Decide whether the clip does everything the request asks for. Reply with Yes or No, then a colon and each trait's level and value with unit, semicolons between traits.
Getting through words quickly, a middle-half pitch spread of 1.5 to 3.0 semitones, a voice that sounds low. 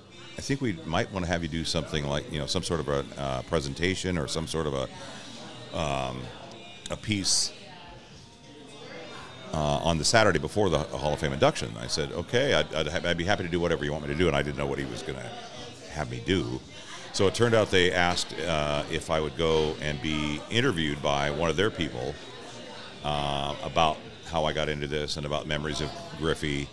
Yes: fast, 215 wpm; average, 2.7 semitones; very low, 75 Hz